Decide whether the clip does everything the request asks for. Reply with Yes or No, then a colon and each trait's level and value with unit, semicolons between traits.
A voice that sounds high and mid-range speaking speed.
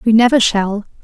Yes: high, 220 Hz; average, 175 wpm